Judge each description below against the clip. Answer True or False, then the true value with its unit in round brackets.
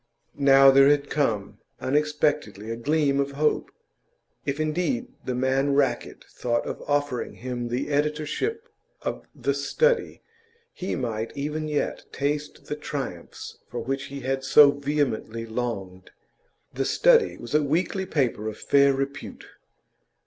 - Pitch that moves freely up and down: False (3.3 semitones)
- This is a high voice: False (140 Hz)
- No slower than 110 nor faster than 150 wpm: True (135 wpm)